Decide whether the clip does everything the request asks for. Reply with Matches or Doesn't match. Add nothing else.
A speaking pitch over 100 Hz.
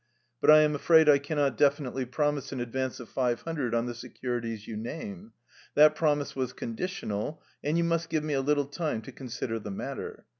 Matches